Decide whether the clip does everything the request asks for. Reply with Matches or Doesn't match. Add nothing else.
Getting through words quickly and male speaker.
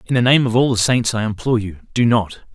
Matches